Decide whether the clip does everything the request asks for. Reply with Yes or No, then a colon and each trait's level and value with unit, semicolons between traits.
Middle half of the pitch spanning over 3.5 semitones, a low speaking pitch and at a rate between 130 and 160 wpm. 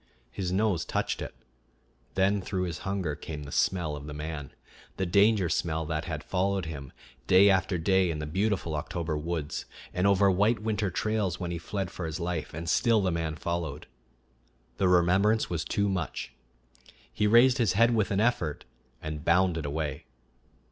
No: average, 3.9 semitones; very low, 90 Hz; average, 175 wpm